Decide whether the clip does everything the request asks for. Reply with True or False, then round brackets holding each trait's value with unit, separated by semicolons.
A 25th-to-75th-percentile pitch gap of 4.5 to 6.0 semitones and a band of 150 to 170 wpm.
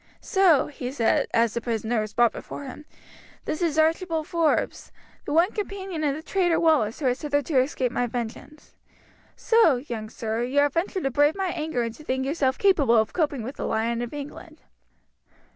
False (5.1 semitones; 190 wpm)